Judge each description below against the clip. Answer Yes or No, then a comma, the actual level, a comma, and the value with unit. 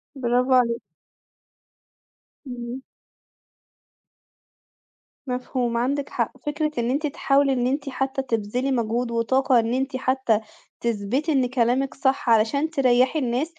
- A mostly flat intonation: Yes, narrow, 2.3 semitones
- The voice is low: No, very high, 255 Hz